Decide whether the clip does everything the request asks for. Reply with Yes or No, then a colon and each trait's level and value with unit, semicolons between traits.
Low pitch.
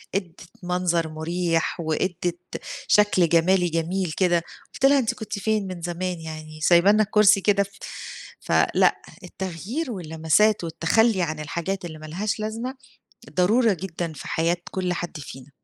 No: medium, 180 Hz